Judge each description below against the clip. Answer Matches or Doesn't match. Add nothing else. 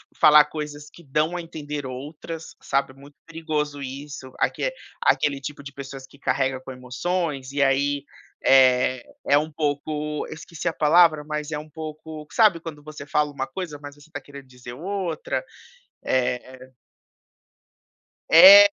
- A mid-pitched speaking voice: Matches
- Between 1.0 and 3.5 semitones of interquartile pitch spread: Matches